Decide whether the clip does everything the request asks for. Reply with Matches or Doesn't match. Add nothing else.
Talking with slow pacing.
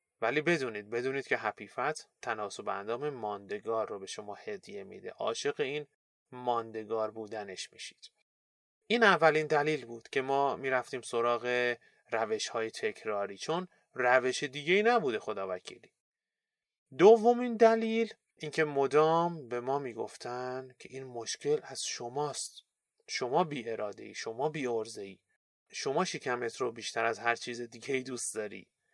Doesn't match